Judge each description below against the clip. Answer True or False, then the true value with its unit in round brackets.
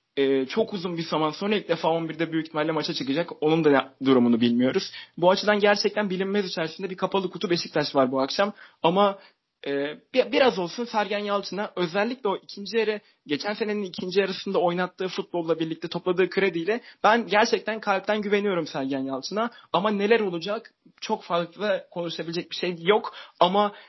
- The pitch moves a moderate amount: True (4.1 semitones)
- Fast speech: True (160 wpm)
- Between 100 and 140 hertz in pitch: False (190 Hz)